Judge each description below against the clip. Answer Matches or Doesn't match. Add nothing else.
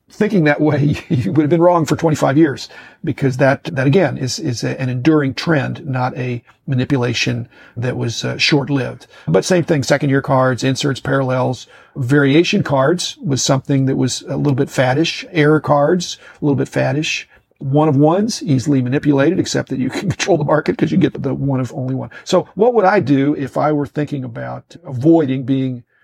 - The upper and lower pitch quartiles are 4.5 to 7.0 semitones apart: Doesn't match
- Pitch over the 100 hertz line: Matches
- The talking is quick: Doesn't match